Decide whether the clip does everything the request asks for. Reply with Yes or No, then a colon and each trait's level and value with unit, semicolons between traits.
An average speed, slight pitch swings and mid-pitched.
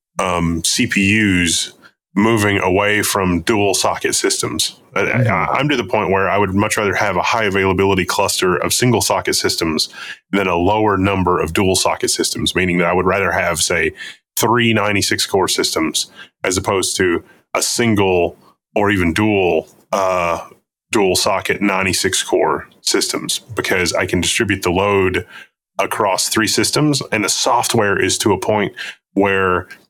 No: average, 155 wpm; narrow, 2.2 semitones; very low, 95 Hz